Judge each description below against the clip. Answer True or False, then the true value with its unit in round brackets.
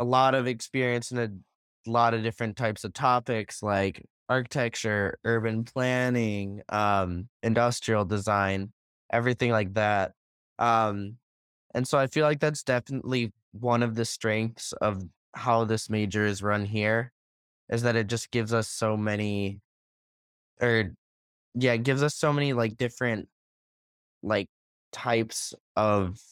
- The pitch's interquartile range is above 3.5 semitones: False (2.8 semitones)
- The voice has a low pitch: True (115 Hz)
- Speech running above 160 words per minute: False (140 wpm)